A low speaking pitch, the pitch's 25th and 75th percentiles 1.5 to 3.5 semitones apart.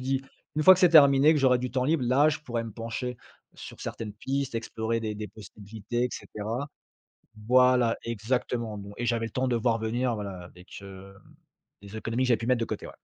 Yes: low, 120 Hz; average, 2.8 semitones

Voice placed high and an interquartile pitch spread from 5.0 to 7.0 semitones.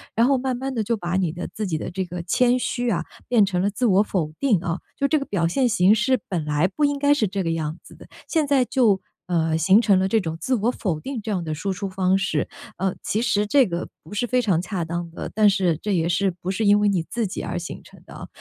Yes: high, 195 Hz; average, 5.3 semitones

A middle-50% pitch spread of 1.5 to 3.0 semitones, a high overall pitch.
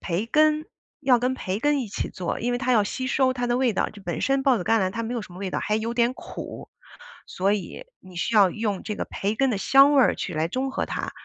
No: average, 4.7 semitones; high, 230 Hz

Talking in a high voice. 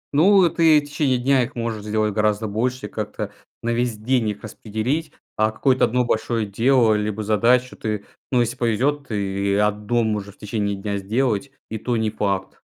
No: low, 110 Hz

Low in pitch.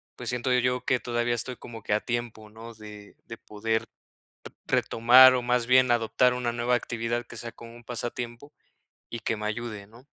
Yes: low, 120 Hz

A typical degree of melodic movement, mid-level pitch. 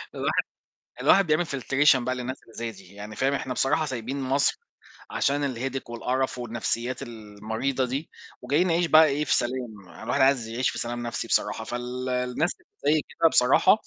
No: average, 3.0 semitones; low, 130 Hz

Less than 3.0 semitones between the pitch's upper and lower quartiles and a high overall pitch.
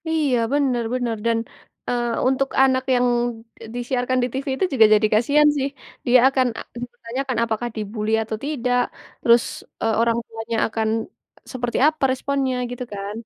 Yes: narrow, 2.5 semitones; high, 245 Hz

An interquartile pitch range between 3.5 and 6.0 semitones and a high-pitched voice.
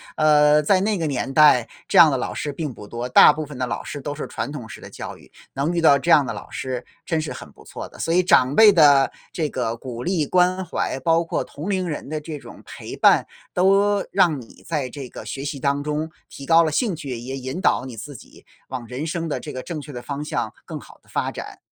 No: average, 3.9 semitones; medium, 150 Hz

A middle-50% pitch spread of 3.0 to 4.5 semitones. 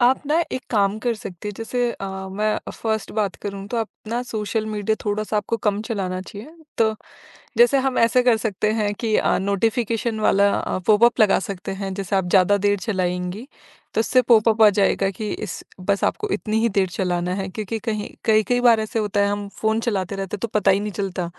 No: narrow, 2.5 semitones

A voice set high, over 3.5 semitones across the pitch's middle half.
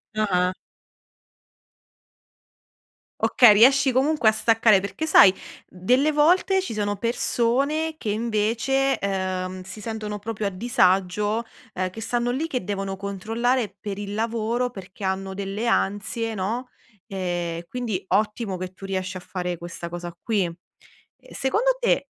Yes: high, 210 Hz; average, 4.3 semitones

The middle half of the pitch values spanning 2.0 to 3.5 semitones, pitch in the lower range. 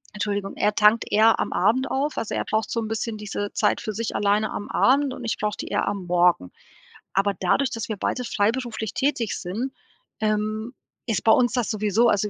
No: narrow, 2.5 semitones; high, 215 Hz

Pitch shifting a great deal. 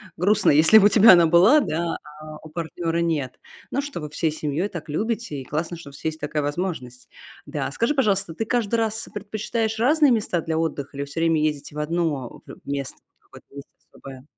Yes: wide, 6.1 semitones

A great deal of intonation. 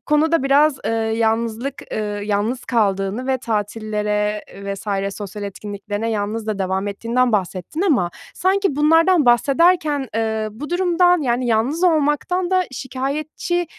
Yes: wide, 6.3 semitones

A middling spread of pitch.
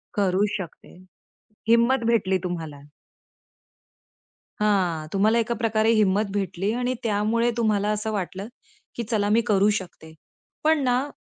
Yes: average, 3.3 semitones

